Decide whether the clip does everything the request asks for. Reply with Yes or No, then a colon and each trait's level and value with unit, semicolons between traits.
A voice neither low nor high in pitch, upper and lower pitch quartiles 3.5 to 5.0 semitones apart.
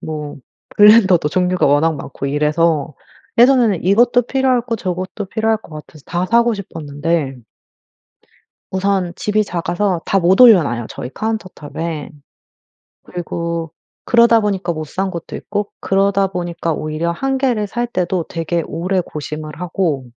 Yes: medium, 180 Hz; average, 4.6 semitones